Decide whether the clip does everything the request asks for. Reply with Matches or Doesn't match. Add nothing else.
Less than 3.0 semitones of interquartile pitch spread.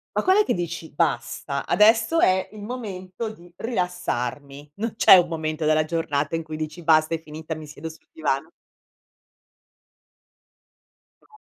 Doesn't match